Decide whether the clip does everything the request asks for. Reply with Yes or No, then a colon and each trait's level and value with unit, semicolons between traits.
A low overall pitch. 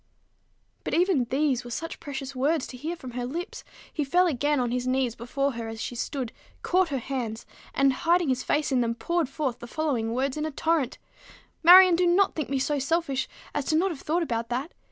No: very high, 275 Hz